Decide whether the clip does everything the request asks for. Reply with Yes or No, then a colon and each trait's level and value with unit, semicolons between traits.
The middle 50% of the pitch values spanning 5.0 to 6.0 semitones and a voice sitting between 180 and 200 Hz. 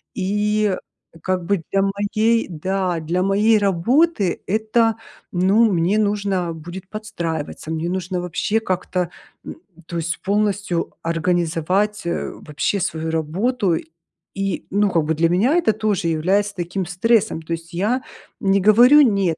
No: average, 3.6 semitones; high, 190 Hz